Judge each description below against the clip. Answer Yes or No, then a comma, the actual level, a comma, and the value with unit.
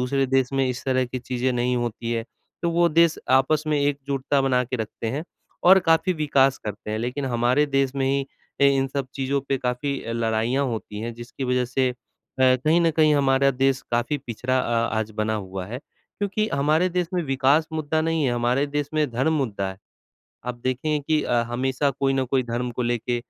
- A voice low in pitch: Yes, low, 130 Hz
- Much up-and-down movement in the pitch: No, average, 3.0 semitones